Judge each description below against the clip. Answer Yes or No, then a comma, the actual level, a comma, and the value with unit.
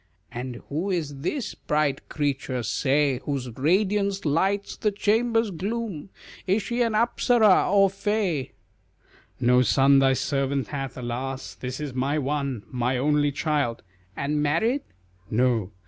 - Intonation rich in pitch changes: Yes, wide, 7.0 semitones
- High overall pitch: No, medium, 145 Hz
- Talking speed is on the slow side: Yes, slow, 130 wpm